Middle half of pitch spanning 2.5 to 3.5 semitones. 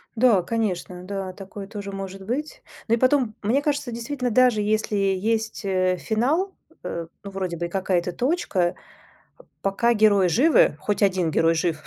No: average, 4.1 semitones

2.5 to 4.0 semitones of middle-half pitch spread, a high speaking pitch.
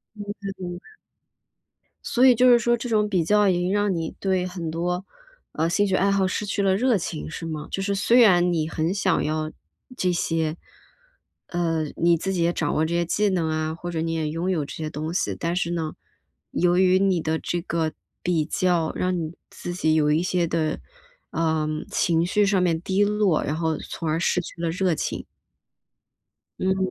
No: average, 2.9 semitones; medium, 175 Hz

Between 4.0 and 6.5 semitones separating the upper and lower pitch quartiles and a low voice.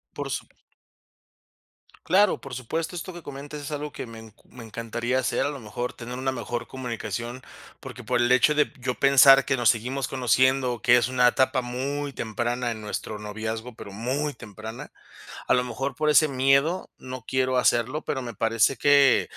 No: average, 2.8 semitones; low, 125 Hz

